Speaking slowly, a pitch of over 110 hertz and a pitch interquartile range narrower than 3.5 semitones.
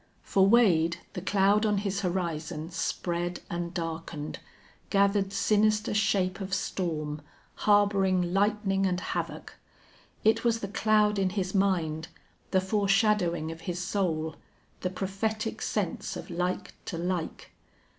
Yes: slow, 125 wpm; high, 190 Hz; average, 3.0 semitones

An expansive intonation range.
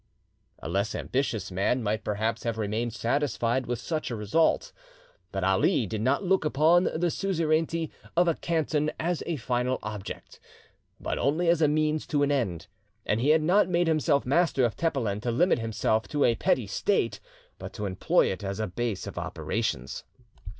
Yes: wide, 6.5 semitones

